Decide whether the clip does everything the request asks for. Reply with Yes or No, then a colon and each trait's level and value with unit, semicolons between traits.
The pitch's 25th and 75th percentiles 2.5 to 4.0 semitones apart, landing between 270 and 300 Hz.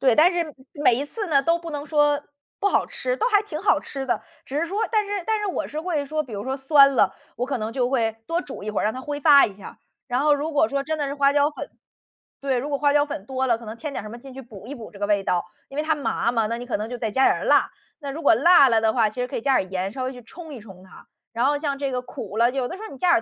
No: average, 4.4 semitones; very high, 275 Hz